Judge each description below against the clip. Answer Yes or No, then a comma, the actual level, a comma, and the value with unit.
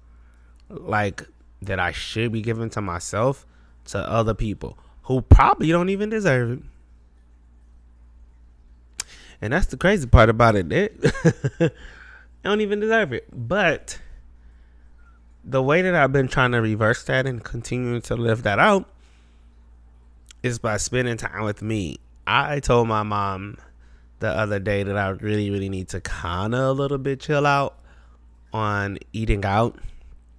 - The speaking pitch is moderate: No, low, 105 Hz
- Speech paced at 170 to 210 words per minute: No, average, 145 wpm